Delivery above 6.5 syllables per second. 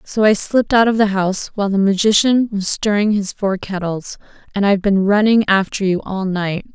No: 5.4 syllables/s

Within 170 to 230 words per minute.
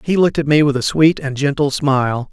No: fast, 260 wpm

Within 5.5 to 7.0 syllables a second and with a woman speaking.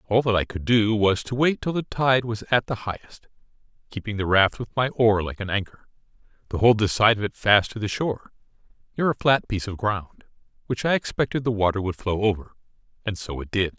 No: 5.7 syllables/s; male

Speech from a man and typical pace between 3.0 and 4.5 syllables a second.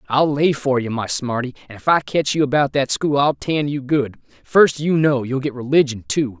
No: male; 5.0 syllables/s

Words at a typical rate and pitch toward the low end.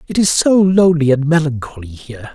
No: average, 180 wpm; medium, 150 Hz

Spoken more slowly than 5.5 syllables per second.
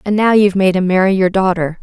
No: 6.4 syllables/s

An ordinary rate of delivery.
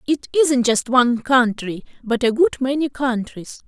Yes: average, 165 wpm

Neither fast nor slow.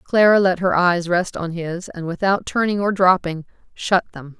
Yes: average, 190 wpm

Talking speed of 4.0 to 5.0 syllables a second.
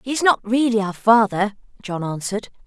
No: 5.5 syllables/s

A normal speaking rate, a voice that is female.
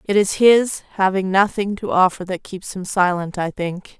Yes: average, 195 wpm; female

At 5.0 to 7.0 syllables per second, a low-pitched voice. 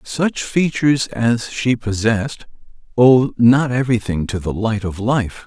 No: 4.1 syllables/s; low, 120 Hz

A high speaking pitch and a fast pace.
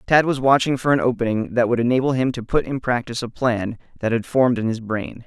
No: low, 120 Hz; fast, 250 wpm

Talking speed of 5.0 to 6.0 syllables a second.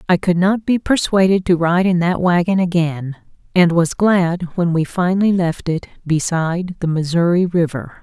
No: 4.7 syllables/s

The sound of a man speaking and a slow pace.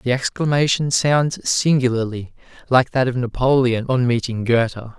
Yes: male; slow, 130 wpm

